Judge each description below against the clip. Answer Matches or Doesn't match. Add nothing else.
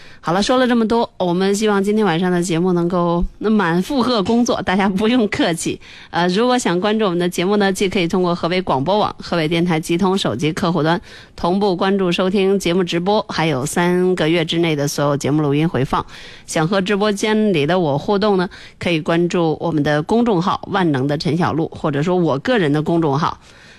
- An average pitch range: Matches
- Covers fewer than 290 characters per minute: Doesn't match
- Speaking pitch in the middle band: Matches